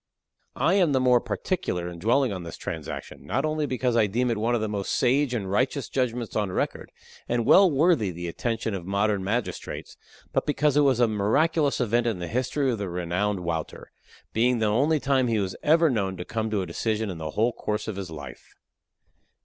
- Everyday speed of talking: No, fast, 210 wpm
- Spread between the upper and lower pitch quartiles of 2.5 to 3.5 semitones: No, average, 5.0 semitones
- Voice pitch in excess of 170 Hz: No, low, 115 Hz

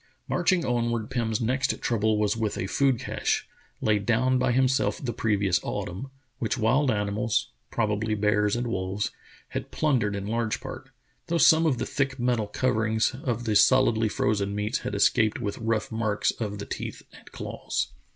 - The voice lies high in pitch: No, low, 110 Hz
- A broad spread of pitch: No, average, 3.2 semitones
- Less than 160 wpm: No, average, 175 wpm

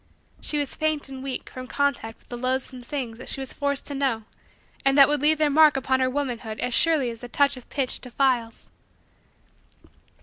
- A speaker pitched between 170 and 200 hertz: No, very high, 265 Hz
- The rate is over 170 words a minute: Yes, average, 200 wpm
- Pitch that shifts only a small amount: Yes, narrow, 2.3 semitones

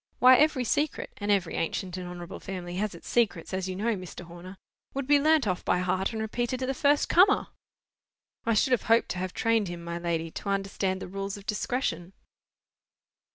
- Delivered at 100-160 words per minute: No, average, 200 wpm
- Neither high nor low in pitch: No, high, 195 Hz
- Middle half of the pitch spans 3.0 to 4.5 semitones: No, average, 5.1 semitones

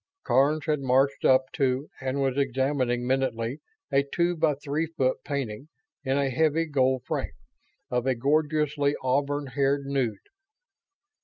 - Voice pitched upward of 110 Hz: Yes, medium, 140 Hz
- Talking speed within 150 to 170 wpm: No, average, 140 wpm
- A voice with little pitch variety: Yes, narrow, 2.0 semitones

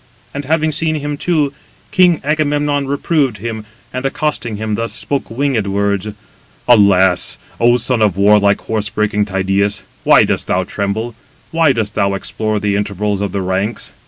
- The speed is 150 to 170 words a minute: Yes, average, 160 wpm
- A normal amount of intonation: No, wide, 5.9 semitones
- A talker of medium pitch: No, low, 110 Hz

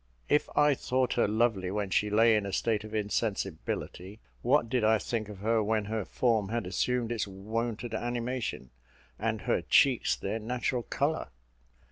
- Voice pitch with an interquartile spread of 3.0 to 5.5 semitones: No, narrow, 2.6 semitones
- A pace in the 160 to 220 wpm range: Yes, average, 165 wpm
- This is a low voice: Yes, low, 110 Hz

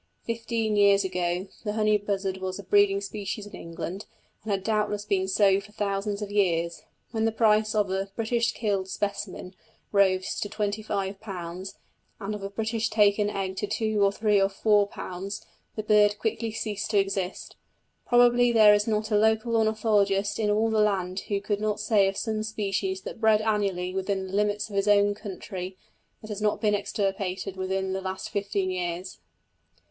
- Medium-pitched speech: No, high, 205 Hz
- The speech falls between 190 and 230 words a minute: No, average, 180 wpm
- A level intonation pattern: Yes, narrow, 1.8 semitones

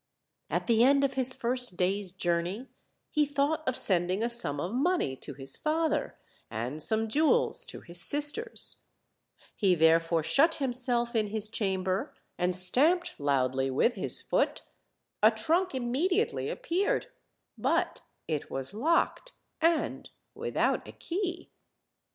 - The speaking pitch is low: No, high, 240 Hz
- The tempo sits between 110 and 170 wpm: Yes, average, 140 wpm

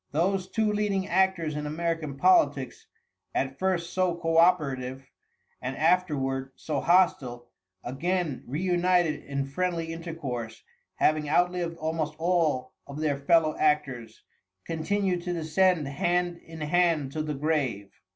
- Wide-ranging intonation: No, average, 4.1 semitones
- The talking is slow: Yes, slow, 125 wpm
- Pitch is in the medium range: Yes, medium, 160 Hz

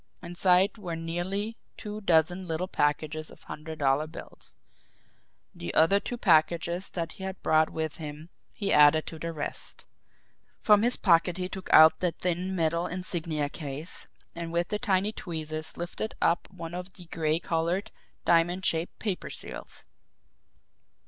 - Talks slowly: No, average, 150 wpm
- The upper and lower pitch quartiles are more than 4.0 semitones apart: No, average, 2.7 semitones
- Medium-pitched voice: Yes, medium, 170 Hz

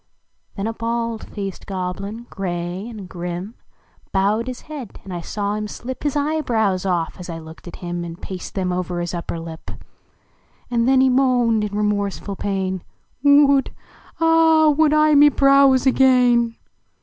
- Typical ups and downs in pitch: No, wide, 6.1 semitones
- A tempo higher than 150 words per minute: Yes, average, 165 wpm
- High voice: Yes, high, 215 Hz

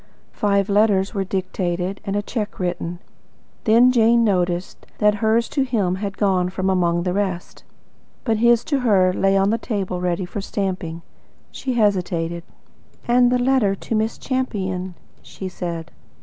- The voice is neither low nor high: No, high, 195 Hz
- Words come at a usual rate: Yes, average, 160 wpm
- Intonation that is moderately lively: Yes, average, 3.5 semitones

